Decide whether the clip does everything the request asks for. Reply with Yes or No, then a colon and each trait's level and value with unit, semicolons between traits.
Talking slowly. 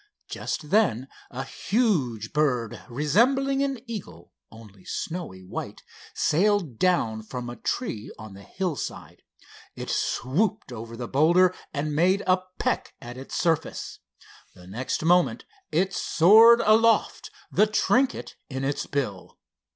Yes: slow, 130 wpm